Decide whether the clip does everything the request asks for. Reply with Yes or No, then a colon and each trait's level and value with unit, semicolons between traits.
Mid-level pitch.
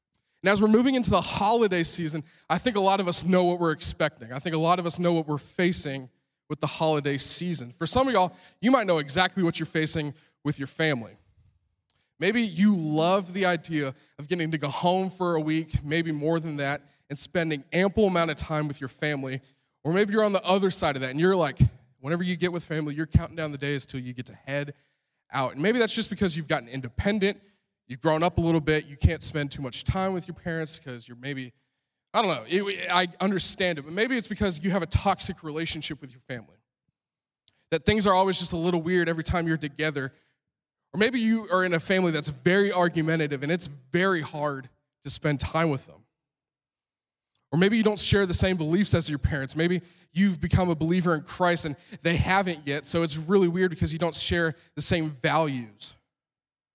Yes: medium, 165 Hz